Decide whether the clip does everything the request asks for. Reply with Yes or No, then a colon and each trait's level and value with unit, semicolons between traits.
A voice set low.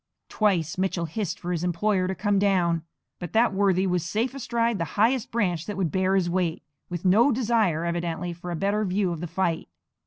No: medium, 185 Hz